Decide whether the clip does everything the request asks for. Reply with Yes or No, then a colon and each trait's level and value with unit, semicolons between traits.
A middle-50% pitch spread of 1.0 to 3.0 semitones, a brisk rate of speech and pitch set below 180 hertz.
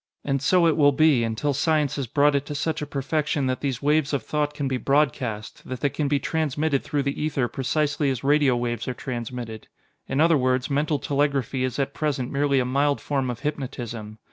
Yes: narrow, 2.5 semitones; fast, 210 wpm; medium, 140 Hz